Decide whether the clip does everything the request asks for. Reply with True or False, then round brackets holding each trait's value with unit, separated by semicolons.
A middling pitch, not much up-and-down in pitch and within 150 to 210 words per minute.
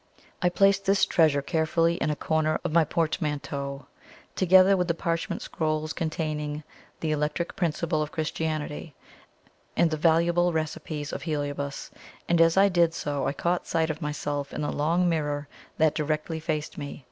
True (160 Hz; 2.1 semitones; 160 wpm)